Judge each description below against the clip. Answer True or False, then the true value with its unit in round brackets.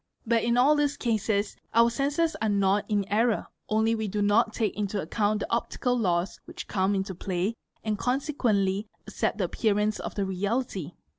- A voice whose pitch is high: True (215 Hz)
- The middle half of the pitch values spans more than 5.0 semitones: False (2.9 semitones)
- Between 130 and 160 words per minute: False (175 wpm)